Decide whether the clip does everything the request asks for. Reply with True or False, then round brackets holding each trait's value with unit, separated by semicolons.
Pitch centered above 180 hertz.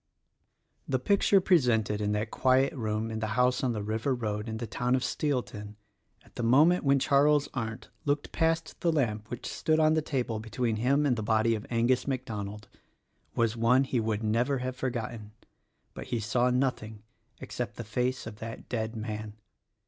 False (120 Hz)